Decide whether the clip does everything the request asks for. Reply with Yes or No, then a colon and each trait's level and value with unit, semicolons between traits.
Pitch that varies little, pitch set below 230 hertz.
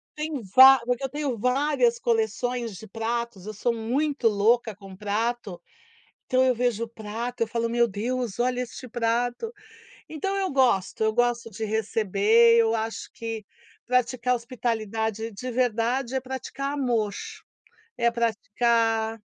No: narrow, 2.3 semitones; high, 235 Hz